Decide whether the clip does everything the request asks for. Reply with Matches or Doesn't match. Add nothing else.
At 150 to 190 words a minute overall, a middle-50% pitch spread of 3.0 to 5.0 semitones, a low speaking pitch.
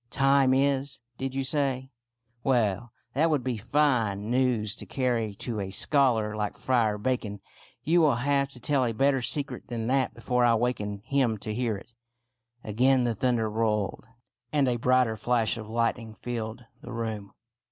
Matches